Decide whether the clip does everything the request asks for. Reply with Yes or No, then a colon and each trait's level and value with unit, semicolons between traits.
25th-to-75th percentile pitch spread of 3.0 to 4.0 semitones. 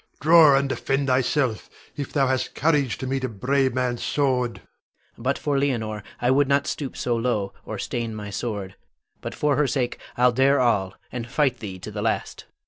Yes: average, 3.3 semitones